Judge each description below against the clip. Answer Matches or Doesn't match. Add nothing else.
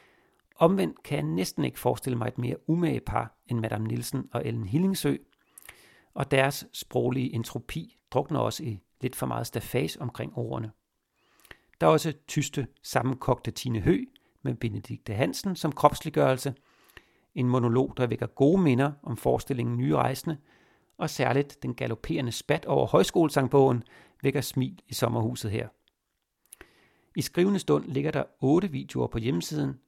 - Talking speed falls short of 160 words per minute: Matches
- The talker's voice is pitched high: Doesn't match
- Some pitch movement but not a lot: Matches